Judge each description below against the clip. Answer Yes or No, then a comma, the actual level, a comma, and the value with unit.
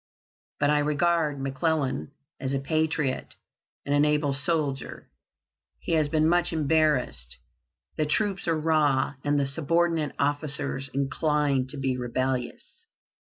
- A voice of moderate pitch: Yes, medium, 145 Hz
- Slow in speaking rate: Yes, slow, 125 wpm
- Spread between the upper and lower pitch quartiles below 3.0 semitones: Yes, narrow, 2.5 semitones